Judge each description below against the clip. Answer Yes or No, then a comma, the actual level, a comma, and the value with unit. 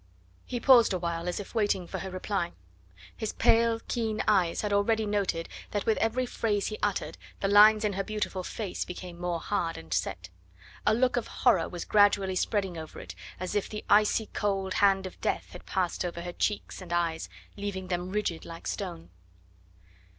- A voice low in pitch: No, high, 195 Hz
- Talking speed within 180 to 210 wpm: Yes, average, 185 wpm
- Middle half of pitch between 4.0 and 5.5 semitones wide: No, average, 3.1 semitones